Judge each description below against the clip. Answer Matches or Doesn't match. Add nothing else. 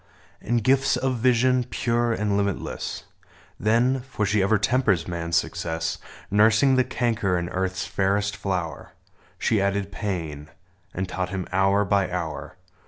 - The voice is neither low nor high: Doesn't match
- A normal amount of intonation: Matches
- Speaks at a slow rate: Doesn't match